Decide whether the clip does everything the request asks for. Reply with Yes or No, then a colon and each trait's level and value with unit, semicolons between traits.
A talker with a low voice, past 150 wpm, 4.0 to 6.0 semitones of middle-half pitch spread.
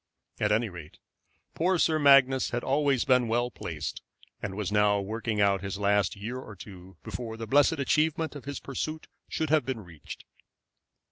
Yes: low, 115 Hz; average, 175 wpm; wide, 5.5 semitones